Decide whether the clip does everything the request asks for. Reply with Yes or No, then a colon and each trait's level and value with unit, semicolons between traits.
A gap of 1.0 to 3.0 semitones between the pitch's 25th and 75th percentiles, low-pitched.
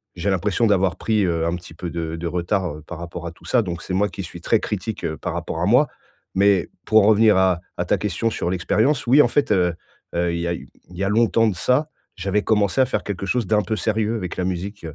No: average, 3.8 semitones; very low, 95 Hz